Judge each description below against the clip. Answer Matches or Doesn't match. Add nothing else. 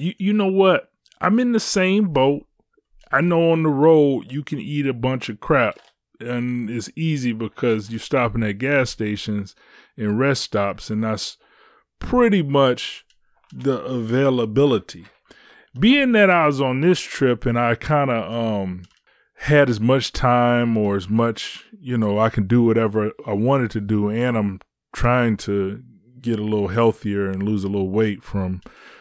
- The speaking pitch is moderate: Doesn't match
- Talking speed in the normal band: Matches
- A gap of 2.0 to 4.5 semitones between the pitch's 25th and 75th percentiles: Doesn't match